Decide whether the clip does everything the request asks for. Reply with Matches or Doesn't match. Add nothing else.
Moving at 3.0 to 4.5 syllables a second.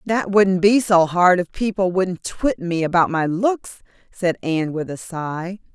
Matches